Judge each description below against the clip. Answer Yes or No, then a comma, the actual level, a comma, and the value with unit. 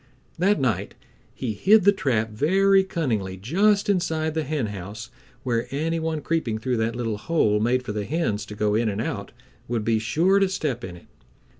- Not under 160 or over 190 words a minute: Yes, average, 185 wpm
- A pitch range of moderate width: No, wide, 7.3 semitones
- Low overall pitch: Yes, low, 125 Hz